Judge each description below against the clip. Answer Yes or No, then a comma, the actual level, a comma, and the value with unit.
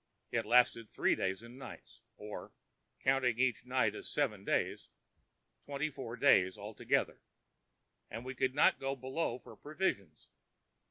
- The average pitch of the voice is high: No, low, 125 Hz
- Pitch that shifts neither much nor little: Yes, average, 3.8 semitones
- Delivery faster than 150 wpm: No, average, 140 wpm